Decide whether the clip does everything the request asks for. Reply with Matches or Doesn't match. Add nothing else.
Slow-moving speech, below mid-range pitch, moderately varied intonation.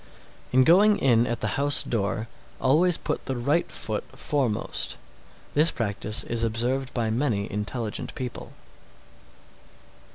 Matches